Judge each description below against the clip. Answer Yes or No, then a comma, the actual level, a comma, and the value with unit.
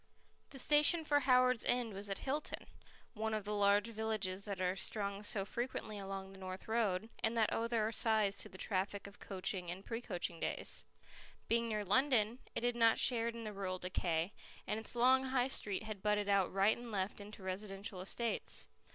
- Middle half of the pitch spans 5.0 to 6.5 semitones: No, average, 3.1 semitones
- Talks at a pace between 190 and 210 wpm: Yes, average, 195 wpm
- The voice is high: Yes, high, 210 Hz